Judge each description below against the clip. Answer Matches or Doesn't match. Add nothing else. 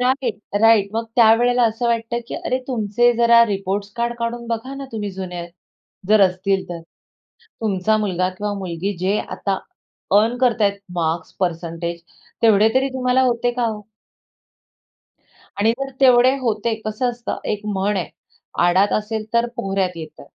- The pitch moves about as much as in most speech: Matches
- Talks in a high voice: Matches